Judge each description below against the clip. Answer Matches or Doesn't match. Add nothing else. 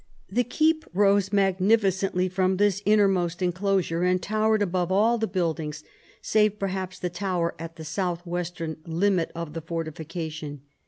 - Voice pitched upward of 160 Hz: Matches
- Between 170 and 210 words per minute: Doesn't match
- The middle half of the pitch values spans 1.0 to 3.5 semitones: Matches